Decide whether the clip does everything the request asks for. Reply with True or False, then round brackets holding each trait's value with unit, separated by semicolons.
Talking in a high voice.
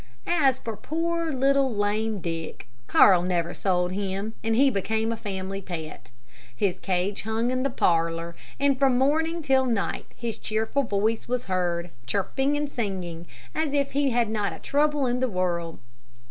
True (220 Hz)